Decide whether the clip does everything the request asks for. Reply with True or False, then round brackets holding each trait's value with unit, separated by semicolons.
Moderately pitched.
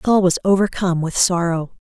True (180 Hz)